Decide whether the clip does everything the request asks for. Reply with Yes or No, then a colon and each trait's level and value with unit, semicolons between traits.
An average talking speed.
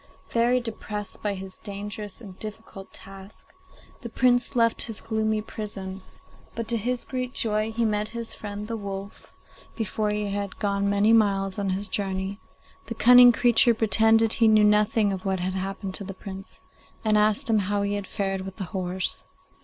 Yes: average, 175 wpm